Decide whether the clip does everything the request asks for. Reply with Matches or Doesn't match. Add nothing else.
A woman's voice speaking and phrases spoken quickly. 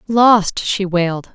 Doesn't match